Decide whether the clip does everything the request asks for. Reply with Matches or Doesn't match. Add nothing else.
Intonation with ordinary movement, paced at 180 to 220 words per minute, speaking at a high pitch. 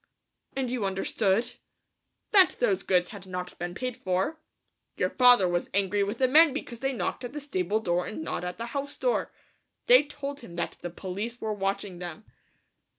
Doesn't match